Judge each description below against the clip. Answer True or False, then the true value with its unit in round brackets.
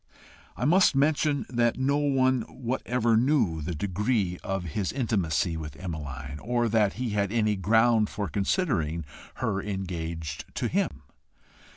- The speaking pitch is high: False (105 Hz)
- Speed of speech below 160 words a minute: True (140 wpm)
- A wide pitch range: True (6.6 semitones)